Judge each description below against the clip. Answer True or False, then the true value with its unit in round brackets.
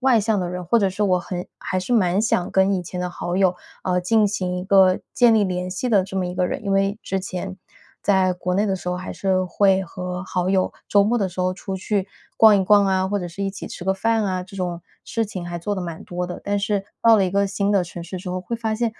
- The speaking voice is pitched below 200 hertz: True (190 Hz)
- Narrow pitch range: True (2.0 semitones)